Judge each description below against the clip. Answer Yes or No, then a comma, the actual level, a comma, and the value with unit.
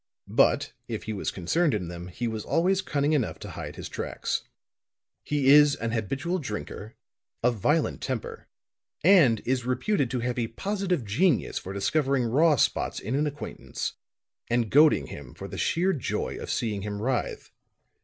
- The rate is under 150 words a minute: No, average, 165 wpm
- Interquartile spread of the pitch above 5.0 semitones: Yes, wide, 5.6 semitones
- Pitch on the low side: Yes, low, 130 Hz